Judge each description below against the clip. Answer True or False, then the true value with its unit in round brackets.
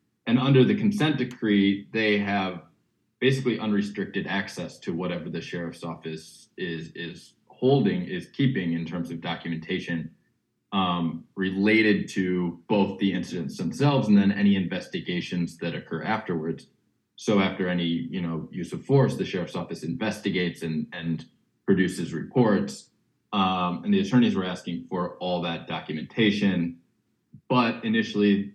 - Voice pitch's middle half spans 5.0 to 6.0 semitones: True (5.5 semitones)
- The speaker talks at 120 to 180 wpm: True (140 wpm)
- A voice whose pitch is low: True (100 Hz)